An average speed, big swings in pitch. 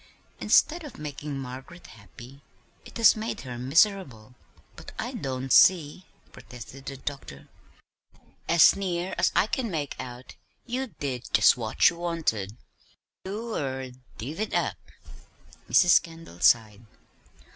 No: slow, 125 wpm; wide, 6.3 semitones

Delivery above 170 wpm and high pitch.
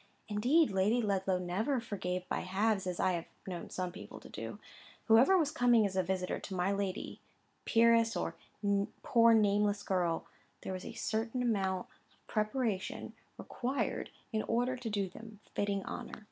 No: average, 160 wpm; high, 205 Hz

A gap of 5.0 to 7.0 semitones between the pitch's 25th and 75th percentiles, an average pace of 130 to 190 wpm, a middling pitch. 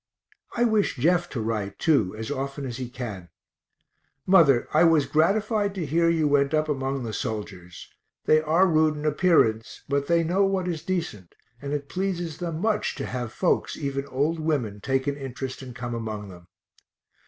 Yes: wide, 5.5 semitones; average, 180 wpm; medium, 145 Hz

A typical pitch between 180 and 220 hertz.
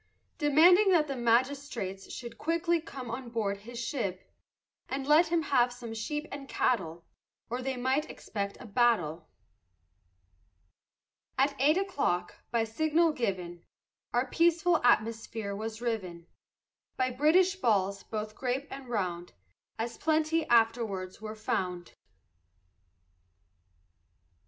No: high, 240 Hz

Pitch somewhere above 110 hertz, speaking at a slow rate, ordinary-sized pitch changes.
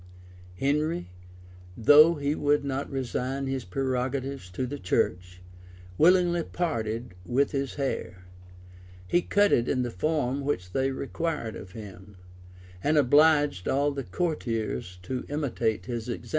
Yes: low, 135 Hz; slow, 130 wpm; average, 4.5 semitones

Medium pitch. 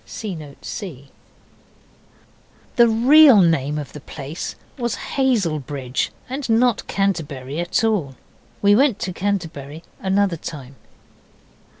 Yes: medium, 175 Hz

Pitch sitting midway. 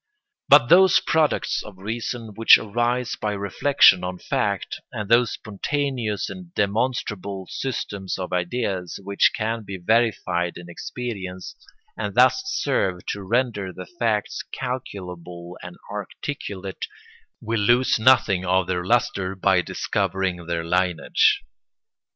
No: low, 100 Hz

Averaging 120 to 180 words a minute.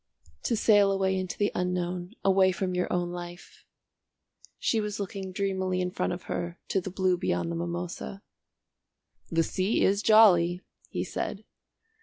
Yes: average, 160 wpm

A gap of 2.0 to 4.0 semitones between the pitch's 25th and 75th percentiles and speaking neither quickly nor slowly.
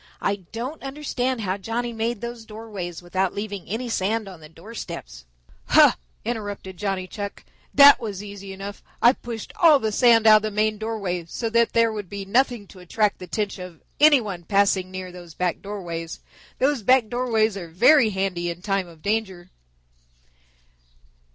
Yes: average, 3.6 semitones; average, 170 wpm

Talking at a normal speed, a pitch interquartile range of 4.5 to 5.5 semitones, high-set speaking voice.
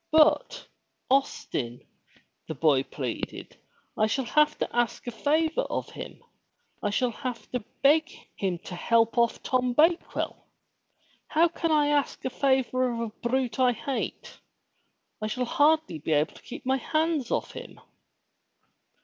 Yes: average, 150 wpm; average, 5.0 semitones; very high, 255 Hz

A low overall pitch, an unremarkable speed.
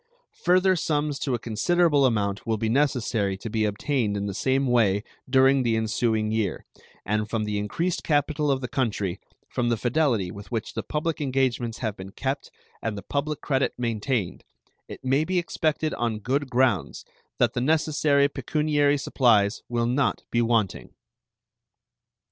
Yes: low, 125 Hz; average, 160 wpm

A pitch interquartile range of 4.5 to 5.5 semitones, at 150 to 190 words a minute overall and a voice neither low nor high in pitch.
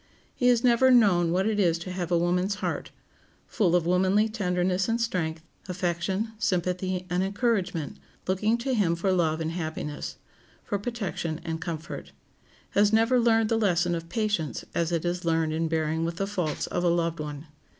No: average, 3.8 semitones; average, 180 wpm; medium, 180 Hz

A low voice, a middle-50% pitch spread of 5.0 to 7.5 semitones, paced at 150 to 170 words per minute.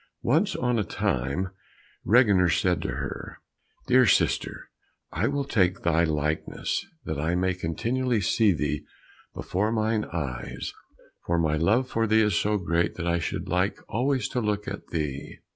Yes: very low, 95 Hz; average, 5.3 semitones; average, 160 wpm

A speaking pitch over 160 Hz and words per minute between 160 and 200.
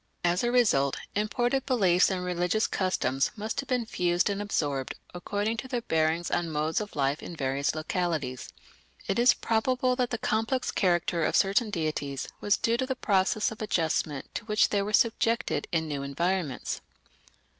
Yes: high, 190 Hz; average, 170 wpm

